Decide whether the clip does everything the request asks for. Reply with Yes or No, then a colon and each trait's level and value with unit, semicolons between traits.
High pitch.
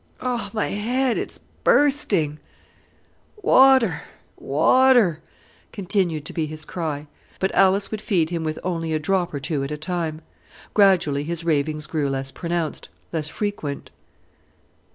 No: medium, 170 Hz